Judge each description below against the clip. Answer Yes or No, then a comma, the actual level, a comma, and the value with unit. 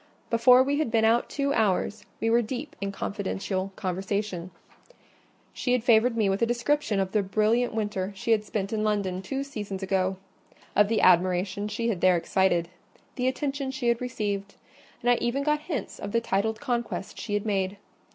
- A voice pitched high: Yes, high, 215 Hz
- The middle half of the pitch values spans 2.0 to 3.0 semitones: No, average, 3.7 semitones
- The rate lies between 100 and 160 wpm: No, average, 180 wpm